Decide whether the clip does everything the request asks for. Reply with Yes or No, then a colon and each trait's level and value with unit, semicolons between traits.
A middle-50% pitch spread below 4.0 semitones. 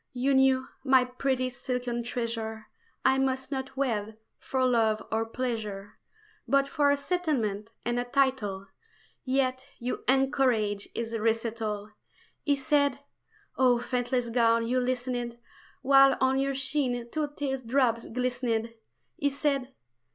Yes: average, 2.7 semitones